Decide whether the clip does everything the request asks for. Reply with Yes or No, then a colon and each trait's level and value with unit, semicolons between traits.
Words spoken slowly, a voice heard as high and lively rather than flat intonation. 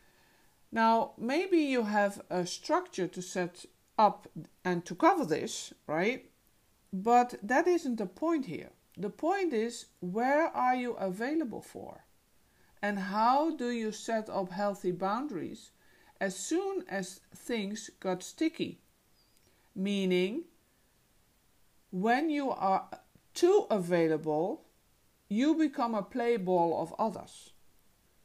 Yes: slow, 115 wpm; high, 220 Hz; wide, 6.8 semitones